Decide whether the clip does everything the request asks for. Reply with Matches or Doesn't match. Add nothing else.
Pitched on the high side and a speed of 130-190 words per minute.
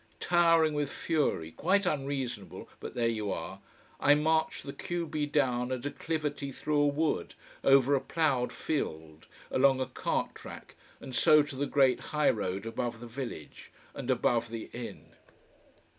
Doesn't match